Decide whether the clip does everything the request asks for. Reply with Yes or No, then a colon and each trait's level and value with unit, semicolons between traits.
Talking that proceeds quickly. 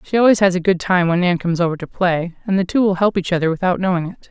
Yes: fast, 305 wpm